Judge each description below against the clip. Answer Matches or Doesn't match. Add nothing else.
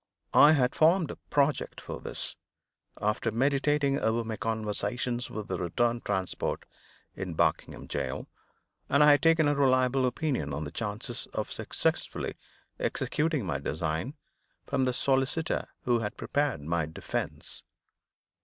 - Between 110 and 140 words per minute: Matches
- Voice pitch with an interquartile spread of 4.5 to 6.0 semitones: Matches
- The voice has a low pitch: Matches